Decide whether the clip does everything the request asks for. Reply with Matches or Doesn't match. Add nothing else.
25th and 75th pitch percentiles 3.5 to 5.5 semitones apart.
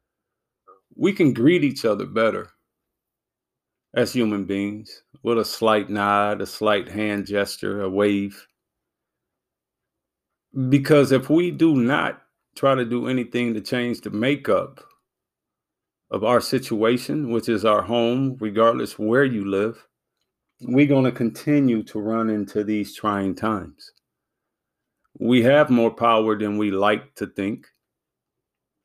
Doesn't match